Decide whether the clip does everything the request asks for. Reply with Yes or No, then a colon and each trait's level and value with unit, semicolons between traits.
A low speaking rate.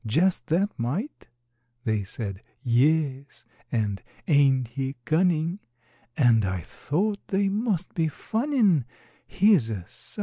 Yes: slow, 115 wpm